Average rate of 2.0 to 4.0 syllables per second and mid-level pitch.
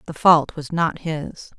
Yes: 3.7 syllables/s; medium, 160 Hz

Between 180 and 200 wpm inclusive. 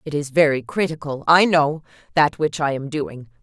No: average, 160 wpm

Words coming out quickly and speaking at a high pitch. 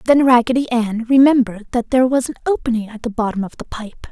Yes: fast, 220 wpm; high, 240 Hz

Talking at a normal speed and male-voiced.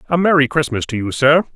No: fast, 230 wpm; male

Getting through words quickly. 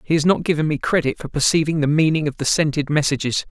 Yes: fast, 240 wpm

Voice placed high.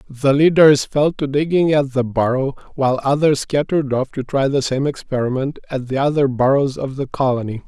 No: low, 135 Hz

